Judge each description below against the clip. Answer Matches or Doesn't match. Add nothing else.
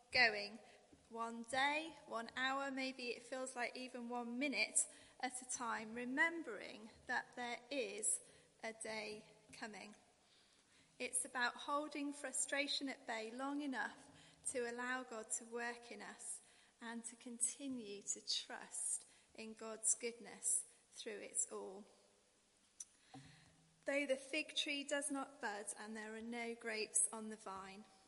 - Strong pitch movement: Doesn't match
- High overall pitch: Matches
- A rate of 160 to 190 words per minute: Doesn't match